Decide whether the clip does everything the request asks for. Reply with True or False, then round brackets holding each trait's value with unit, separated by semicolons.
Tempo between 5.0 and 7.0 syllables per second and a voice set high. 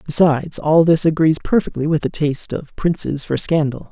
False (5.4 syllables/s; 155 Hz)